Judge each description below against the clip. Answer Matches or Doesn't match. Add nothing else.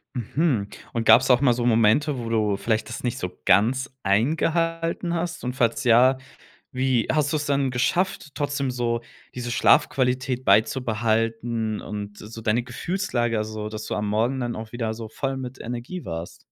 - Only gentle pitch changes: Doesn't match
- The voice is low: Matches